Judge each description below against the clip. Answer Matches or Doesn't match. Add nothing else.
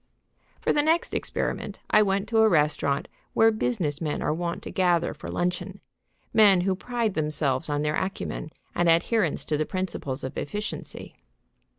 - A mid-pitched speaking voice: Matches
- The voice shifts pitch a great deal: Matches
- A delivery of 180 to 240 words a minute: Doesn't match